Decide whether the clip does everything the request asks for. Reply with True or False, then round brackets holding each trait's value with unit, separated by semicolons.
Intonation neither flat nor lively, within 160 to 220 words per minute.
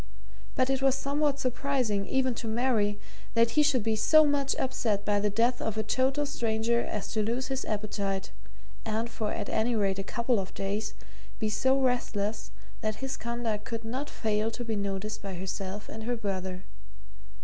True (3.7 semitones; 180 wpm)